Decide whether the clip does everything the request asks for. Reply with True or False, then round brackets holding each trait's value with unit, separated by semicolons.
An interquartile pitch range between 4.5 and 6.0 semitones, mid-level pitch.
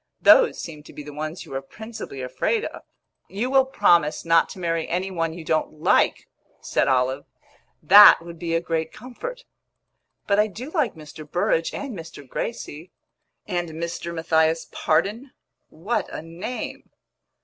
True (5.2 semitones; 170 Hz)